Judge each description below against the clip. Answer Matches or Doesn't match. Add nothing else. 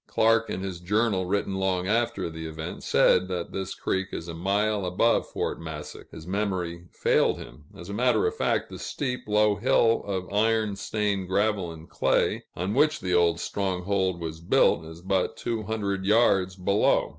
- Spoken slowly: Doesn't match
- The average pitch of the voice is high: Doesn't match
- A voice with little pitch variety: Doesn't match